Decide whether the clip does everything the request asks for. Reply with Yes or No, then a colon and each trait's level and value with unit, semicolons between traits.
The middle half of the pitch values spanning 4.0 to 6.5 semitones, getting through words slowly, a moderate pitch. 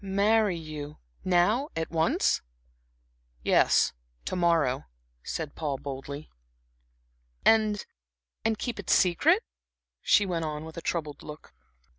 Yes: average, 5.1 semitones; slow, 115 wpm; medium, 170 Hz